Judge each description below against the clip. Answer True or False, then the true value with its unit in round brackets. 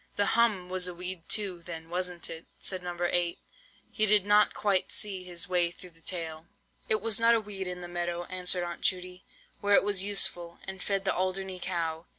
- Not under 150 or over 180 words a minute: False (205 wpm)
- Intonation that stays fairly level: True (2.2 semitones)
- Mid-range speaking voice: True (180 Hz)